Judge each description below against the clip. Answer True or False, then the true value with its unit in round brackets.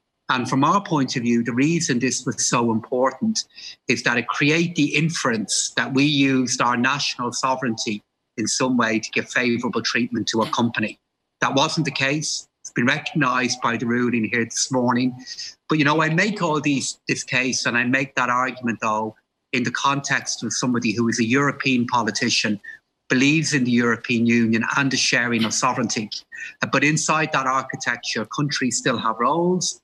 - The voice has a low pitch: True (130 Hz)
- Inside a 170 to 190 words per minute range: True (180 wpm)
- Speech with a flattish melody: False (3.3 semitones)